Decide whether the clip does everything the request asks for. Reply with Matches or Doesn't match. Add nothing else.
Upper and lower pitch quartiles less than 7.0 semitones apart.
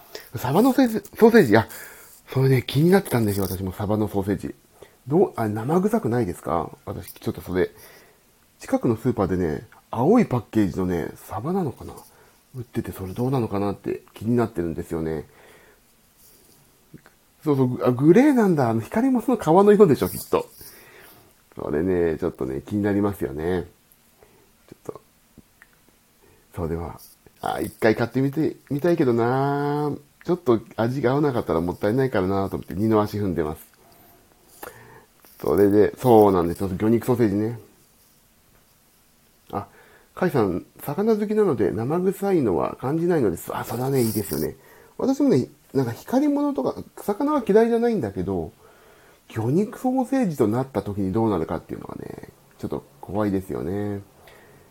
Doesn't match